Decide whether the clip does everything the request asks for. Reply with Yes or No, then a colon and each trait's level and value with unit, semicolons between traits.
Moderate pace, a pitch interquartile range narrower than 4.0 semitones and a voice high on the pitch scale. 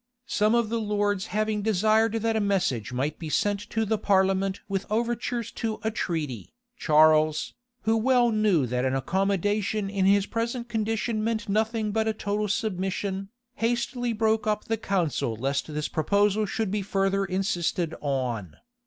Yes: average, 160 wpm; average, 3.6 semitones; high, 205 Hz